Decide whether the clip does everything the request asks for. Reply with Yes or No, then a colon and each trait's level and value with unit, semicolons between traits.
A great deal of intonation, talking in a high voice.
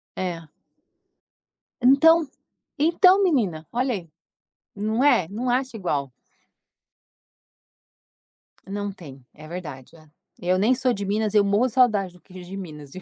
Yes: wide, 6.2 semitones; high, 200 Hz